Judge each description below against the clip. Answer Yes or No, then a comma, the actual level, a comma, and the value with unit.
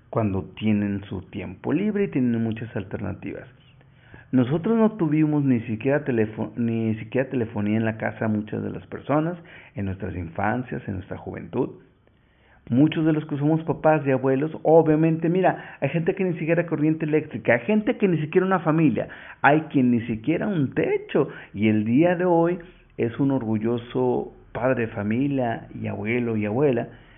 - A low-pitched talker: Yes, low, 130 Hz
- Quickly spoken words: No, average, 170 wpm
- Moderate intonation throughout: No, wide, 6.2 semitones